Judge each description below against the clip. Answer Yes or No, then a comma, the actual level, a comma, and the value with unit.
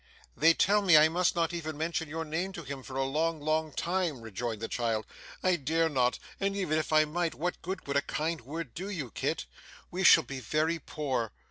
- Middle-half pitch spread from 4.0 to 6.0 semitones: No, average, 3.6 semitones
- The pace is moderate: No, fast, 220 wpm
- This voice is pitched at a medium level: Yes, medium, 155 Hz